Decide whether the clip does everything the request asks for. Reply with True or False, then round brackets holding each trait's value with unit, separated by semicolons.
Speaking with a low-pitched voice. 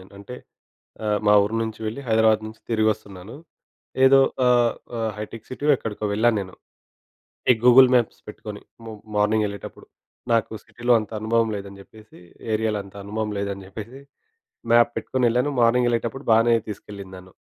True (110 Hz)